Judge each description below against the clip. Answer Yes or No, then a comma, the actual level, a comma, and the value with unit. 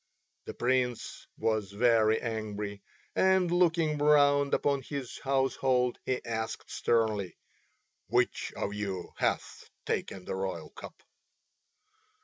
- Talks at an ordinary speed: No, slow, 110 wpm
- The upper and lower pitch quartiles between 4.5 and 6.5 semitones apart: Yes, average, 5.0 semitones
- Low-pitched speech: Yes, low, 120 Hz